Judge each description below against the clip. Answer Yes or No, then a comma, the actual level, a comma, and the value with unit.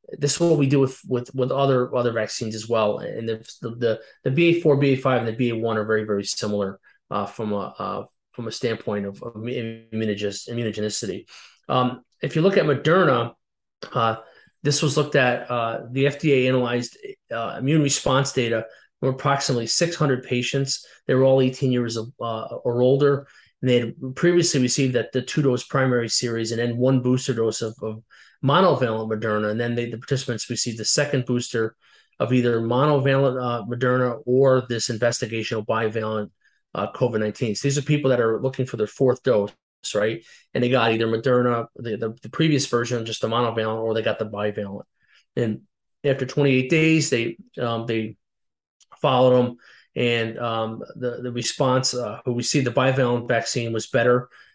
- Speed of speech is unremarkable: Yes, average, 180 wpm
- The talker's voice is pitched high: No, low, 125 Hz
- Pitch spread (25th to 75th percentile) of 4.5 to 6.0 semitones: No, average, 2.9 semitones